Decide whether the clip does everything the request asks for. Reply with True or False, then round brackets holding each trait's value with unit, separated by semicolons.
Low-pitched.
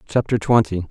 True (105 Hz)